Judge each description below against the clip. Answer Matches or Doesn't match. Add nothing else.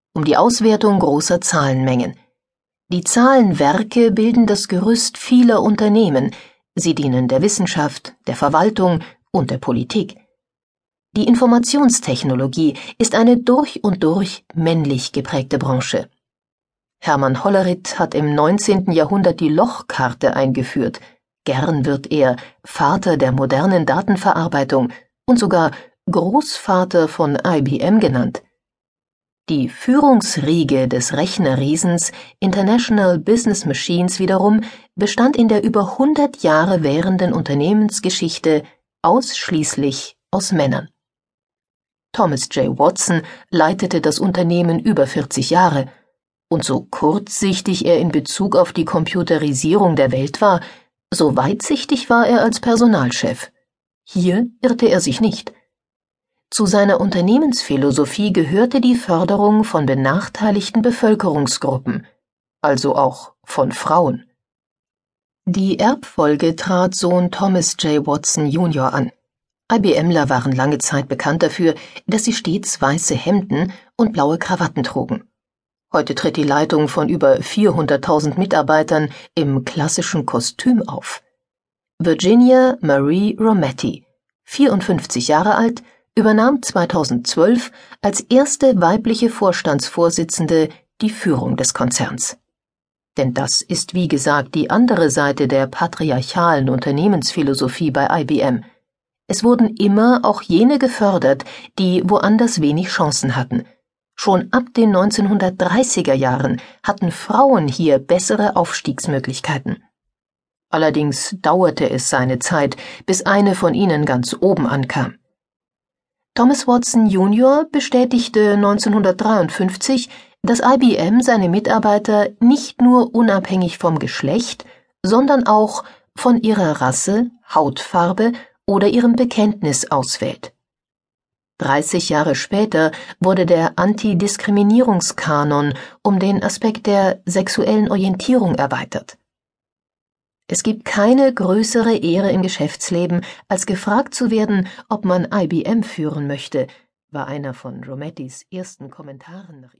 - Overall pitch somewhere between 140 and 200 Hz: Matches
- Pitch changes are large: Matches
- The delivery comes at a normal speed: Doesn't match